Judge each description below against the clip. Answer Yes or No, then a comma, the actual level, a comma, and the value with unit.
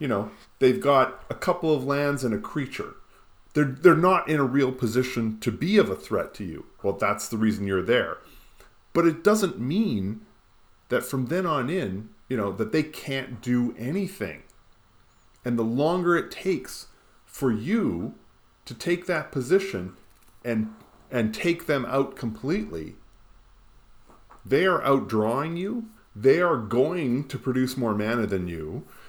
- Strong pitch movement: Yes, wide, 7.0 semitones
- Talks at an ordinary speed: Yes, average, 160 wpm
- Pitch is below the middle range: Yes, low, 130 Hz